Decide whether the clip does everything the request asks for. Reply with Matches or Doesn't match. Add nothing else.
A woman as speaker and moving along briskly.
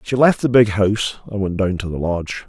Doesn't match